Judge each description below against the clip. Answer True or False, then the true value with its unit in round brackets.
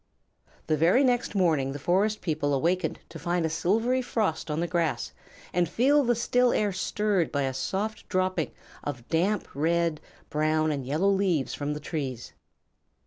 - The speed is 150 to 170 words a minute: True (165 wpm)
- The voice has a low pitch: False (170 Hz)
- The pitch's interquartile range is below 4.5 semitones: False (5.0 semitones)